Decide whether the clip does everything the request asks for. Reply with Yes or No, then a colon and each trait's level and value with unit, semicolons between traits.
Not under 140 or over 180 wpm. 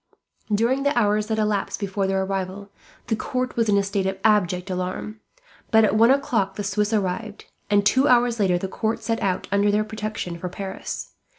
No: average, 195 wpm